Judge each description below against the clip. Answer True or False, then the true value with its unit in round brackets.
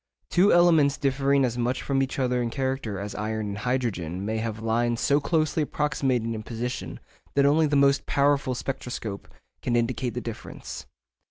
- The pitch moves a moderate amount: True (3.6 semitones)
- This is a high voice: False (125 Hz)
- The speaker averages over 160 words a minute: True (170 wpm)